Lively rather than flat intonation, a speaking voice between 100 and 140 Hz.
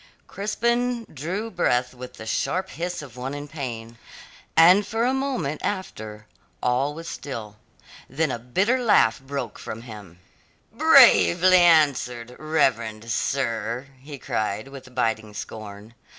Yes: wide, 7.2 semitones; low, 135 Hz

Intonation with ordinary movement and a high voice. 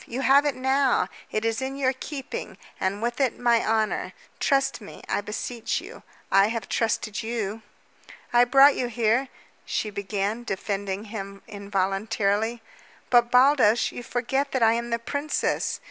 Yes: average, 3.8 semitones; high, 230 Hz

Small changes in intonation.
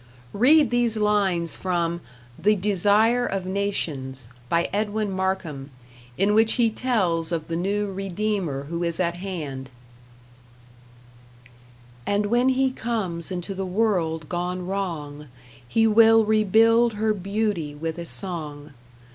No: average, 4.2 semitones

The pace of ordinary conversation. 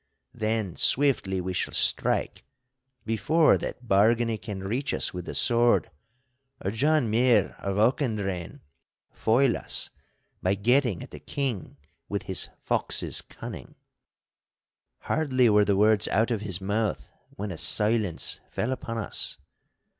No: slow, 130 wpm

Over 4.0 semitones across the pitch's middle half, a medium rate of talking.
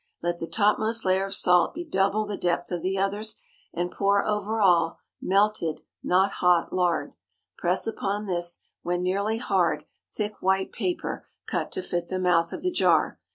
No: average, 3.0 semitones; average, 160 wpm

